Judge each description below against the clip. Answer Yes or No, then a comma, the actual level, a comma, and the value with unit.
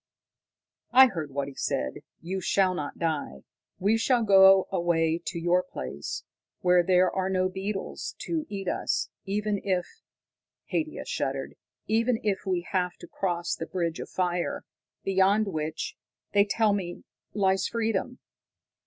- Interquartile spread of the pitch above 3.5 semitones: No, average, 2.9 semitones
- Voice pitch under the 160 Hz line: No, high, 190 Hz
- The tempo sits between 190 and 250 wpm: No, average, 145 wpm